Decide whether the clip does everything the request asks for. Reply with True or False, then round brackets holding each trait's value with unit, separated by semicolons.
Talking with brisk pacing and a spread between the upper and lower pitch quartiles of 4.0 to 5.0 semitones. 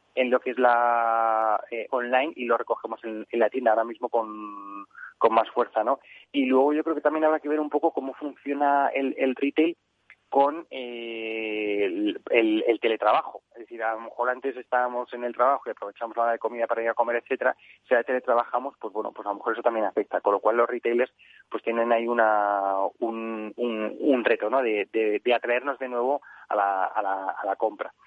False (220 wpm; 3.0 semitones)